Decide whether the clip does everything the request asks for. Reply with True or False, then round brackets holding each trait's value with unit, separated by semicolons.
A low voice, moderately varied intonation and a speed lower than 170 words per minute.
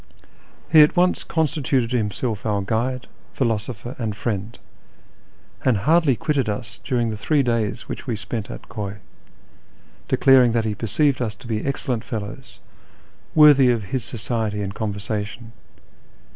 True (115 Hz; 3.8 semitones; 140 wpm)